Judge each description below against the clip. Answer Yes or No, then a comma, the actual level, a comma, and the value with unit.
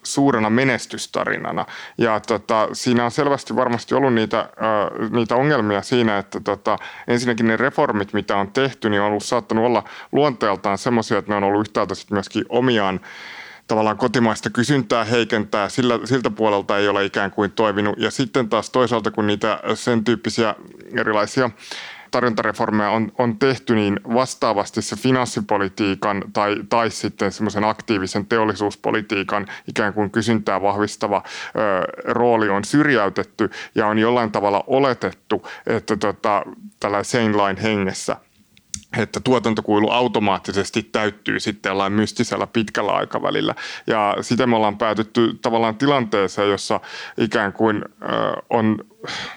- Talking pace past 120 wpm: Yes, average, 135 wpm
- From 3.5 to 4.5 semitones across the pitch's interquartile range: No, average, 2.9 semitones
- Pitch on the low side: Yes, low, 110 Hz